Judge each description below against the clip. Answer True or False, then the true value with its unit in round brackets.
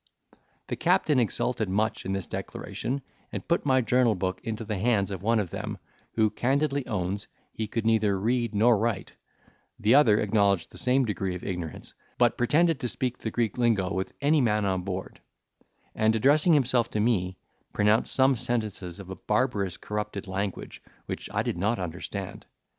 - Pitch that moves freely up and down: False (3.9 semitones)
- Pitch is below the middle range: True (110 Hz)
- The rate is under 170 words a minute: False (175 wpm)